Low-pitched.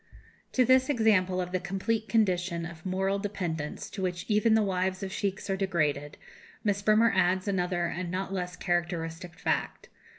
No: medium, 185 Hz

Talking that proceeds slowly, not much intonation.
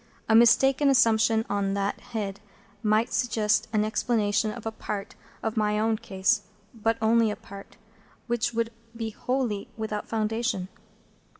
Yes: slow, 130 wpm; narrow, 1.6 semitones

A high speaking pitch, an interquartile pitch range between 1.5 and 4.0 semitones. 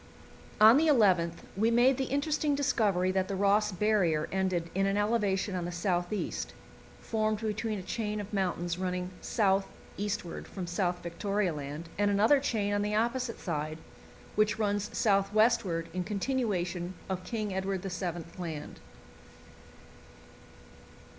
Yes: high, 200 Hz; average, 3.3 semitones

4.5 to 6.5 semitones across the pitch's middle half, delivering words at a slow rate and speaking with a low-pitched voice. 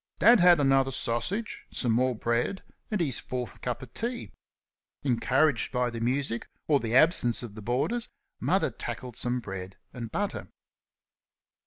No: average, 4.9 semitones; average, 150 wpm; low, 125 Hz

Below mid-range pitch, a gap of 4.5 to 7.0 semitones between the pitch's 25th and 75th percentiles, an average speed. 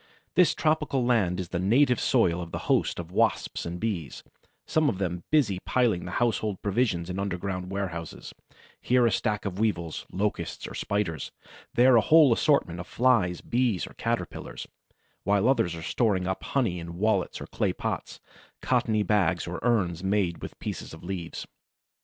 Yes: low, 100 Hz; average, 5.1 semitones; average, 165 wpm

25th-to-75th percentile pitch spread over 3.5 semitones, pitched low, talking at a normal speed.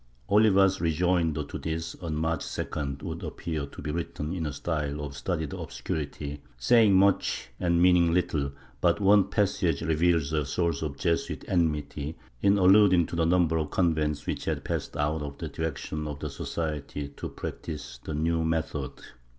No: average, 2.9 semitones; very low, 80 Hz; average, 165 wpm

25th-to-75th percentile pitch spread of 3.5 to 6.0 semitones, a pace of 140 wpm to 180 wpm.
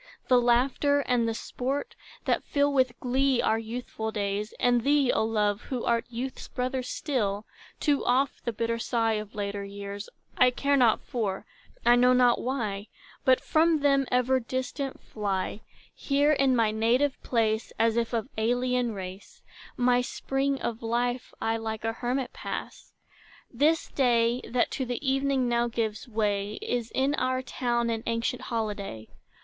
No: average, 2.8 semitones; average, 160 wpm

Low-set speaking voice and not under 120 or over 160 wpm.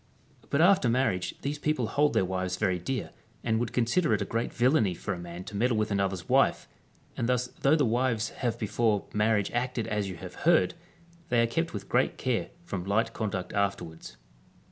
No: low, 115 Hz; average, 200 wpm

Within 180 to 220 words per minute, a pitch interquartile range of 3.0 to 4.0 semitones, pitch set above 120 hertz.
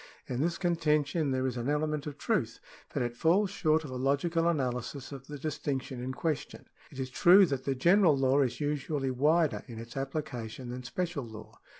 Yes: average, 200 wpm; average, 3.5 semitones; medium, 140 Hz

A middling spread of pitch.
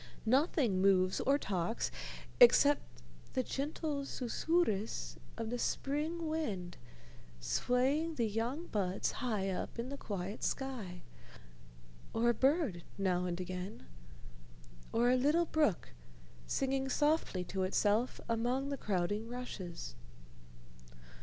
No: wide, 6.5 semitones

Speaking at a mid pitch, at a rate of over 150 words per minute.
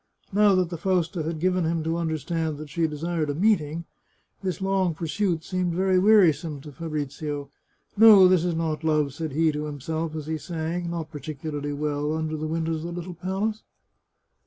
Yes: medium, 160 Hz; average, 195 wpm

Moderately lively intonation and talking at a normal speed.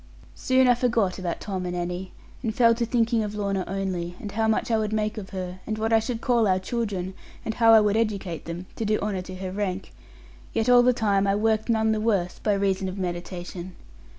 No: average, 3.2 semitones; fast, 230 wpm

